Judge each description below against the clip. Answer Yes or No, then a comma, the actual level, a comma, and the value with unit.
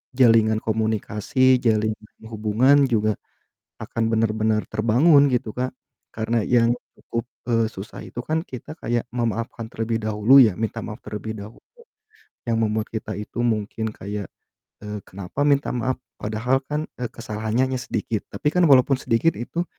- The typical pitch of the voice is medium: No, low, 115 Hz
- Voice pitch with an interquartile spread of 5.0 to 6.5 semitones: No, average, 2.7 semitones